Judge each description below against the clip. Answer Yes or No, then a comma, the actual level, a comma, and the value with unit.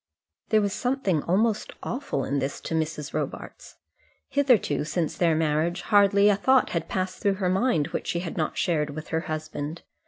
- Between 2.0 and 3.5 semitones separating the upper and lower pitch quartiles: No, average, 4.6 semitones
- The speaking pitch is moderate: Yes, medium, 175 Hz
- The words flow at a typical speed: Yes, average, 180 wpm